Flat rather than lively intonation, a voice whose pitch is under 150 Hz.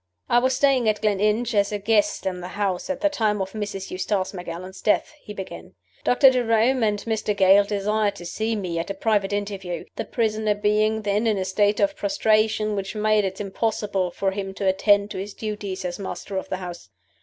No: narrow, 2.1 semitones; high, 205 Hz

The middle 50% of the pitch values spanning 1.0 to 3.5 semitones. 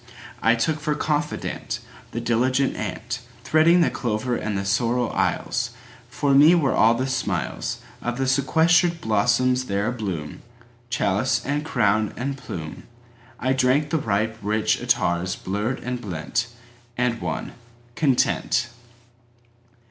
Yes: average, 3.0 semitones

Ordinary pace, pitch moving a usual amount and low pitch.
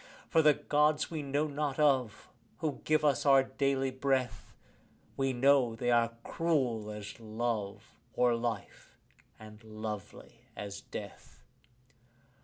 No: slow, 125 wpm; average, 4.5 semitones; low, 130 Hz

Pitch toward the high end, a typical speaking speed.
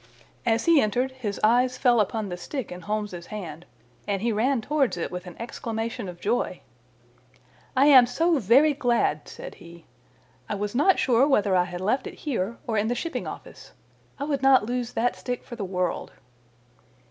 Yes: high, 230 Hz; average, 185 wpm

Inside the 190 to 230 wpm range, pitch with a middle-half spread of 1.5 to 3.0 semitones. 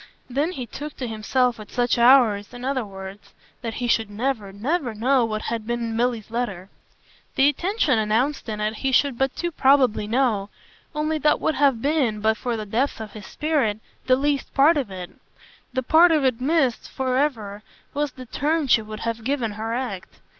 No: average, 195 wpm; average, 4.1 semitones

